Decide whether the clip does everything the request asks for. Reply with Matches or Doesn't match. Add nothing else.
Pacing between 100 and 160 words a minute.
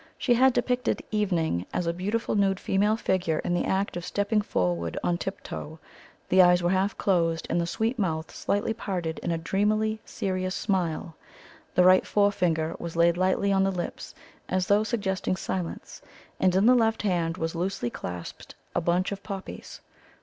Doesn't match